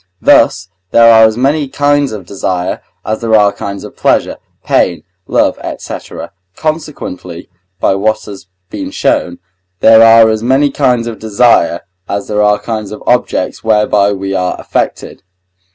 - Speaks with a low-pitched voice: Yes, low, 110 Hz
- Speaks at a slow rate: No, average, 150 wpm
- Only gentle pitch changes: No, average, 3.0 semitones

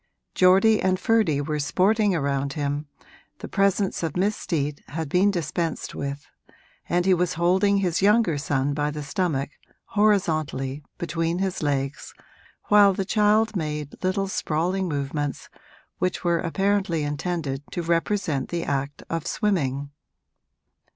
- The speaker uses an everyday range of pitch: Yes, average, 4.9 semitones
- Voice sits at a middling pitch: Yes, medium, 170 Hz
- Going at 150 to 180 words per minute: No, slow, 135 wpm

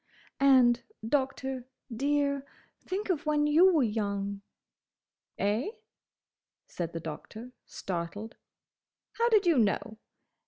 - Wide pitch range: Yes, wide, 6.1 semitones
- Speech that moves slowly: Yes, slow, 95 wpm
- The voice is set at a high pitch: Yes, very high, 255 Hz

